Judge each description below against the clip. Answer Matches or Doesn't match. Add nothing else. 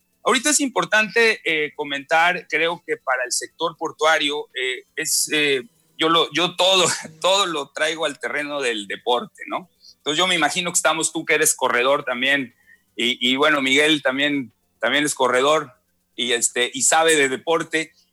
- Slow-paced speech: Doesn't match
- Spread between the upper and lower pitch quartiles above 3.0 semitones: Matches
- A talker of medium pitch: Matches